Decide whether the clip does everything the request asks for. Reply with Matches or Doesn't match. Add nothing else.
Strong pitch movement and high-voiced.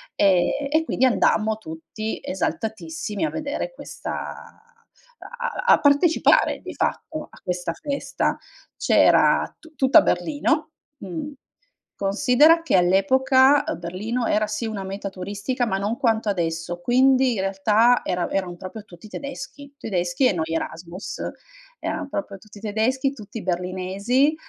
Matches